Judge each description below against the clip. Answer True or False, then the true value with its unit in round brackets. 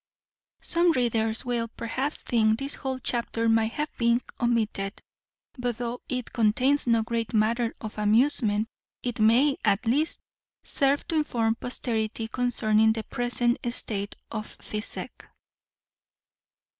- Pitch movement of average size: False (2.1 semitones)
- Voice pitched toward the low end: False (235 Hz)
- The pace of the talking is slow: True (125 wpm)